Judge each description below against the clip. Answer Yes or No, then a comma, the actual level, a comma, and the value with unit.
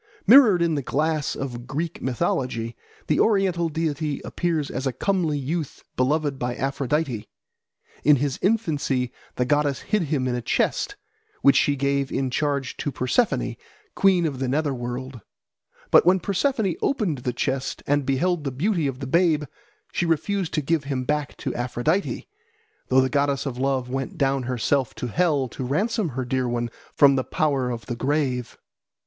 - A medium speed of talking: Yes, average, 170 wpm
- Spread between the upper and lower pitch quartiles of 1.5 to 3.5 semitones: No, average, 4.1 semitones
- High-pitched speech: No, medium, 140 Hz